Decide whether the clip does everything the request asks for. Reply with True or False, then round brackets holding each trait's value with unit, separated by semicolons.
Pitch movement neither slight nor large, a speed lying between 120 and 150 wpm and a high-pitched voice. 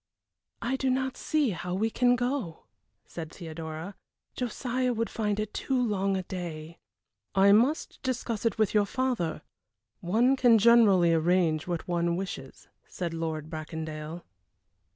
False (6.5 semitones; 140 wpm; 195 Hz)